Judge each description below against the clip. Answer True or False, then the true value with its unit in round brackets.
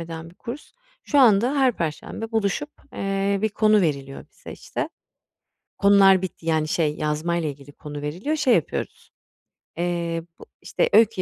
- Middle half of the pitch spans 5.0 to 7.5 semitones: True (5.6 semitones)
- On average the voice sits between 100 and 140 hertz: False (185 Hz)